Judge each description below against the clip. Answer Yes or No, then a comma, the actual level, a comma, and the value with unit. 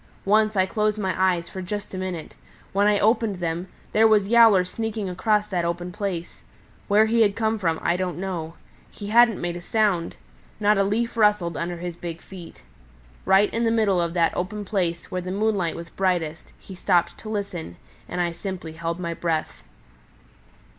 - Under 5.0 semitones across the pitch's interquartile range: Yes, average, 3.5 semitones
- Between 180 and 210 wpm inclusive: Yes, average, 190 wpm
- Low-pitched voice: No, high, 190 Hz